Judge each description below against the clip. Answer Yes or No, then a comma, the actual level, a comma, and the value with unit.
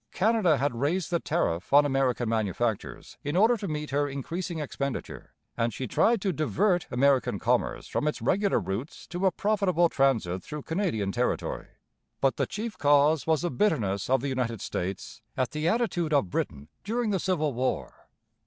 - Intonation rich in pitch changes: Yes, wide, 6.5 semitones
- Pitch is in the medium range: Yes, medium, 145 Hz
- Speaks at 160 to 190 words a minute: Yes, average, 170 wpm